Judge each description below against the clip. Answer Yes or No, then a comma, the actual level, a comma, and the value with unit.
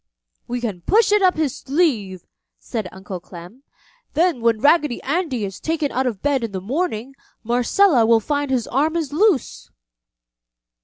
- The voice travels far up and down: Yes, wide, 6.4 semitones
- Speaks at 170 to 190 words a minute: No, average, 160 wpm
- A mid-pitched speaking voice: No, very high, 260 Hz